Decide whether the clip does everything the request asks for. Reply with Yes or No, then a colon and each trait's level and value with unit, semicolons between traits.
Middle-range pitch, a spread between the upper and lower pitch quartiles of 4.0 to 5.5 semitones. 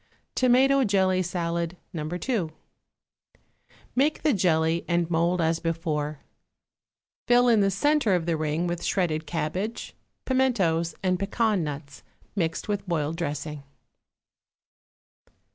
Yes: medium, 175 Hz; average, 4.3 semitones